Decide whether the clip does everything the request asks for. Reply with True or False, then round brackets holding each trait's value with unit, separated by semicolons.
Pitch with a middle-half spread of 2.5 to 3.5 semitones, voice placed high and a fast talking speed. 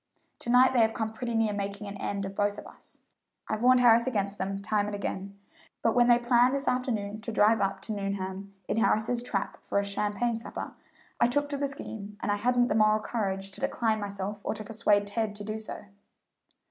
True (2.8 semitones; 215 Hz; 220 wpm)